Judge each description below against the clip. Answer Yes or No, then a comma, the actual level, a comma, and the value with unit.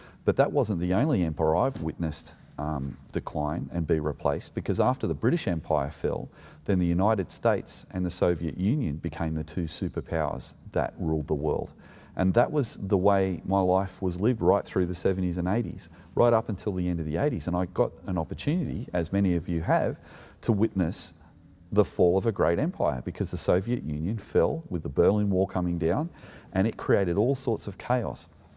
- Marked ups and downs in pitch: No, average, 3.8 semitones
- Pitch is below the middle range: Yes, very low, 90 Hz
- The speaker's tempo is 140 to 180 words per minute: No, average, 195 wpm